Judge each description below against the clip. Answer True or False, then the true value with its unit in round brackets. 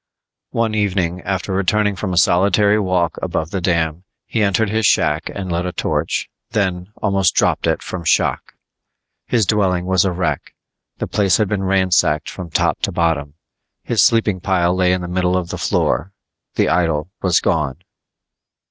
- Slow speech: False (170 wpm)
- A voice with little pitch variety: True (2.3 semitones)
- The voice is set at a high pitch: False (90 Hz)